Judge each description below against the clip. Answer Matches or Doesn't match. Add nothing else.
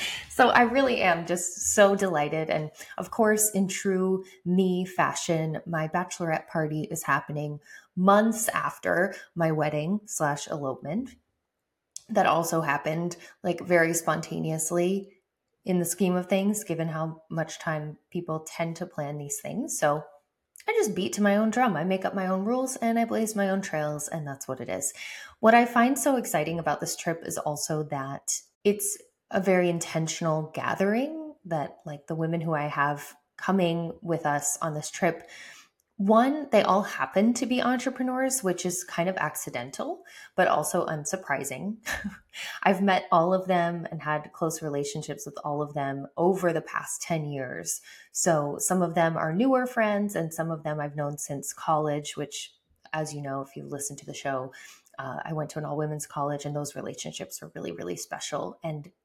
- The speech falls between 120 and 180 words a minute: Matches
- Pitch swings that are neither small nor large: Matches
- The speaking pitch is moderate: Matches